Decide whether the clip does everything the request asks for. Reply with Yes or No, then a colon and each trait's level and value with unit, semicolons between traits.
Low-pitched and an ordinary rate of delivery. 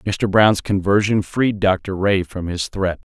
Yes: very low, 95 Hz; average, 170 wpm